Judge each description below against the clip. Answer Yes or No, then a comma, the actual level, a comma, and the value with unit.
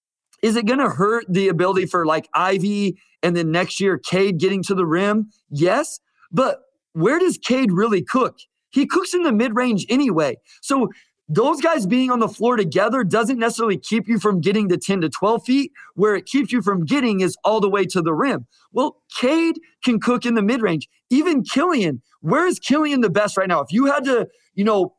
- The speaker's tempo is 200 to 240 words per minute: Yes, fast, 205 wpm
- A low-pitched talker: No, high, 220 Hz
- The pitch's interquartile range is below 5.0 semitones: No, wide, 5.6 semitones